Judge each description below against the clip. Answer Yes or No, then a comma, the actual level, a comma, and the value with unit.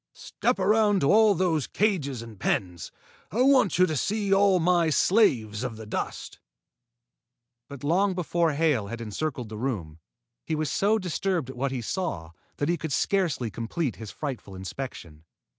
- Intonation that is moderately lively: No, wide, 8.3 semitones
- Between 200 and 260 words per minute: No, average, 165 wpm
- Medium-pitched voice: Yes, medium, 155 Hz